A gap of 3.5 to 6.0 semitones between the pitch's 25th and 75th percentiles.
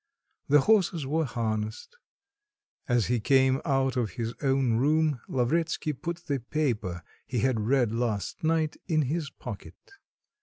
Yes: average, 4.9 semitones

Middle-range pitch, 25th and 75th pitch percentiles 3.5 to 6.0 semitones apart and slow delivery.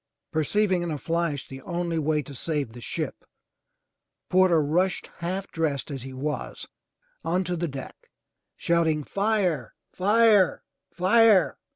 Yes: medium, 170 Hz; average, 3.9 semitones; slow, 130 wpm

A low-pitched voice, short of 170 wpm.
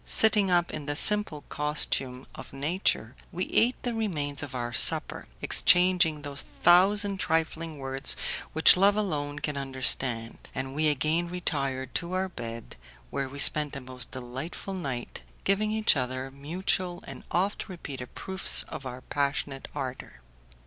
No: medium, 150 Hz; average, 150 wpm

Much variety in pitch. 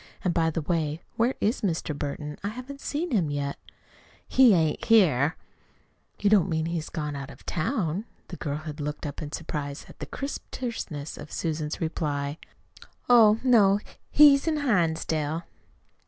Yes: wide, 6.6 semitones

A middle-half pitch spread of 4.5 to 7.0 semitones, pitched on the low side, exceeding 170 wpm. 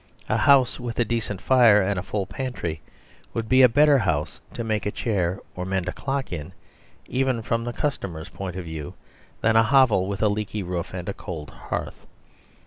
Yes: average, 4.8 semitones; low, 105 Hz; average, 200 wpm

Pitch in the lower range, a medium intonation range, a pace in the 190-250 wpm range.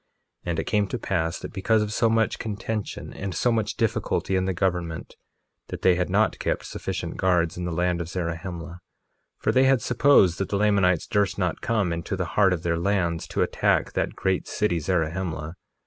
Yes: very low, 95 Hz; average, 3.5 semitones; average, 200 wpm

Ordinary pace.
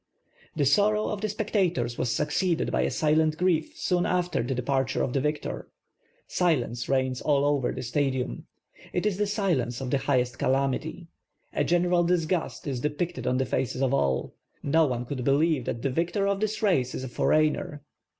Yes: average, 190 wpm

